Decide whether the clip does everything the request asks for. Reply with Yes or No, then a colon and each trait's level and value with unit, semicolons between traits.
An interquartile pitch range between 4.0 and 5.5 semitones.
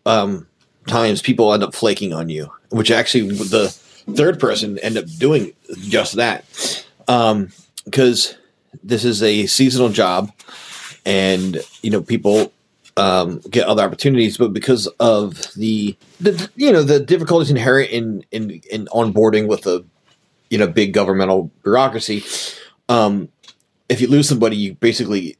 No: average, 3.6 semitones